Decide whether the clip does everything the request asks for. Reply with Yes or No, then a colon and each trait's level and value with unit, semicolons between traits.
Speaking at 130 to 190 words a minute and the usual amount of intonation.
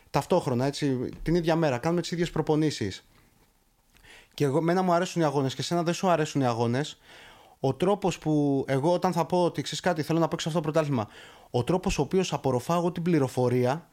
No: fast, 200 wpm; average, 4.1 semitones